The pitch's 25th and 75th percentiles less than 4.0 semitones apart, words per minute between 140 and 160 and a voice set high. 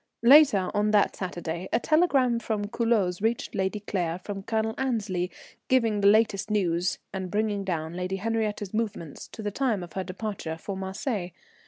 No: average, 3.3 semitones; average, 170 wpm; high, 205 Hz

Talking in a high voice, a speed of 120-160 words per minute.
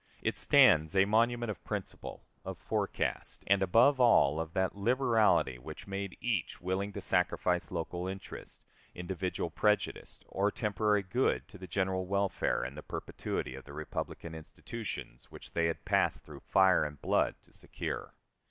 No: very low, 95 Hz; average, 155 wpm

